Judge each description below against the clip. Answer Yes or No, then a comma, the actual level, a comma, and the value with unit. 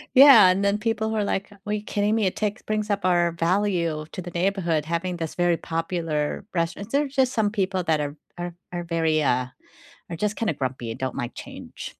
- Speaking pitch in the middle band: Yes, medium, 180 Hz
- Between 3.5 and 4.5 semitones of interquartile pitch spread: Yes, average, 4.1 semitones